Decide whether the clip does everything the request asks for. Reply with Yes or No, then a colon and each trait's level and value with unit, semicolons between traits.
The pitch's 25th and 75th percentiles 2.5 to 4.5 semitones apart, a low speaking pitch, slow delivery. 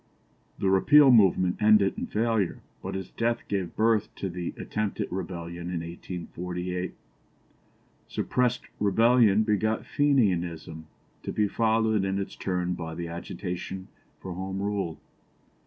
Yes: average, 3.5 semitones; very low, 95 Hz; slow, 125 wpm